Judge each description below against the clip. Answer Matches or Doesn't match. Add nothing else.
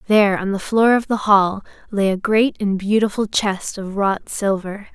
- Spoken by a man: Doesn't match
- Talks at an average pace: Matches